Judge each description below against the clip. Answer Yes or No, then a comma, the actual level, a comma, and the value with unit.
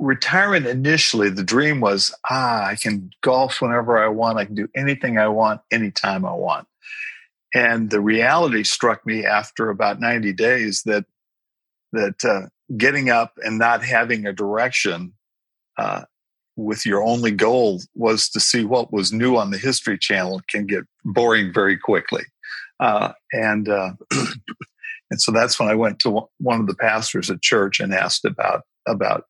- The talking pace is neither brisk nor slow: Yes, average, 165 wpm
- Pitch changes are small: No, average, 3.2 semitones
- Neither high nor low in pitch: No, low, 115 Hz